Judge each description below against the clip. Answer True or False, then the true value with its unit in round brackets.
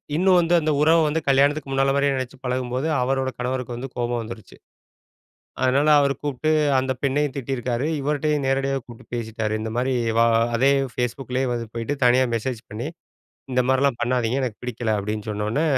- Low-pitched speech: True (130 Hz)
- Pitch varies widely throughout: False (2.7 semitones)